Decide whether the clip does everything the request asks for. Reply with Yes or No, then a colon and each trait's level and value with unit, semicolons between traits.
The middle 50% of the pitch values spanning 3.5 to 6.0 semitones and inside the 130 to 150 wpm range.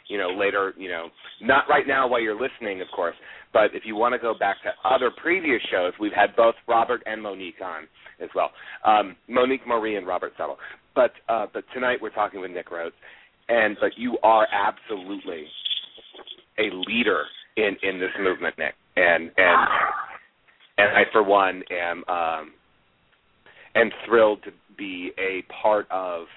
No: average, 3.8 semitones; average, 170 wpm